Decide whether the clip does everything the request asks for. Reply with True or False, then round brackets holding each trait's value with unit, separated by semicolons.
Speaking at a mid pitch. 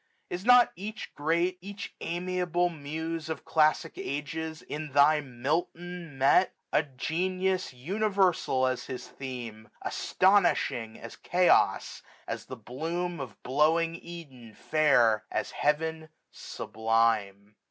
True (155 Hz)